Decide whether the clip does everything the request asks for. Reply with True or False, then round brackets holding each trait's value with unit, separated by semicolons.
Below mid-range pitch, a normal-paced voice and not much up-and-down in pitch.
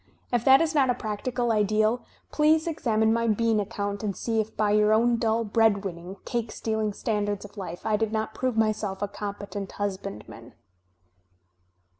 False (220 Hz; 170 wpm; 2.2 semitones)